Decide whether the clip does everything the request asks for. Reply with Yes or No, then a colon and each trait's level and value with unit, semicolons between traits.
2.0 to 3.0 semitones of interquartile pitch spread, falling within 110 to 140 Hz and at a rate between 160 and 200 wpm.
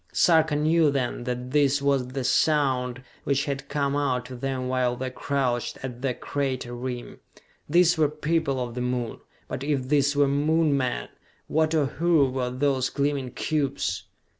Yes: narrow, 2.5 semitones; low, 135 Hz; average, 165 wpm